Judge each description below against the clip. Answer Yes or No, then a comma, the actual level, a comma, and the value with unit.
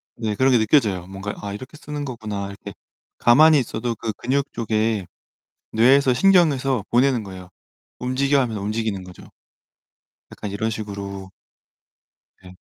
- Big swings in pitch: No, average, 4.7 semitones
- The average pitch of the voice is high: No, low, 115 Hz